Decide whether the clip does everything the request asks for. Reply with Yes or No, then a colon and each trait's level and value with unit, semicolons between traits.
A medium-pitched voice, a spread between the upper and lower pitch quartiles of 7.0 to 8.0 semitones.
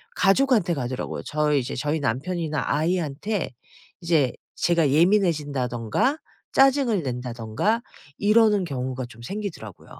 Yes: medium, 155 Hz; wide, 7.5 semitones